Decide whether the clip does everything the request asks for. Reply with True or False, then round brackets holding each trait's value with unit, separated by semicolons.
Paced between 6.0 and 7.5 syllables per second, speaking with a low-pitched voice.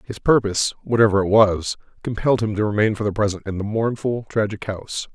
True (6.1 syllables/s; 105 Hz)